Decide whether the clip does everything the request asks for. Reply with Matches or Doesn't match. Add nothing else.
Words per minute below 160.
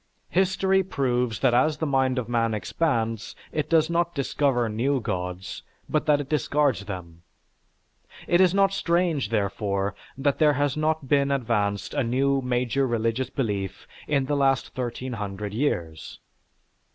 Matches